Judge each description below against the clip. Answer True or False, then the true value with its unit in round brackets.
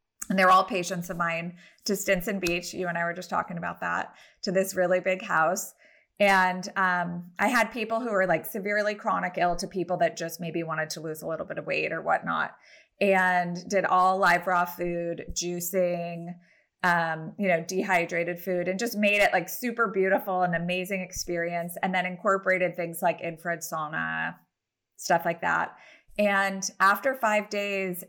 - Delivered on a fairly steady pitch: True (2.1 semitones)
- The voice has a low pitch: False (185 Hz)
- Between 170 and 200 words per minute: True (180 wpm)